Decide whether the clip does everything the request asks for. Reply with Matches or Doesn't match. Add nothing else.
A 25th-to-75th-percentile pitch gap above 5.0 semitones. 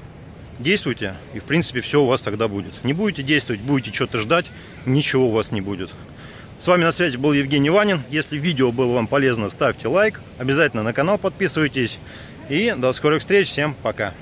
Matches